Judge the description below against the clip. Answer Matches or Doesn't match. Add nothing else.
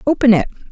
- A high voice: Matches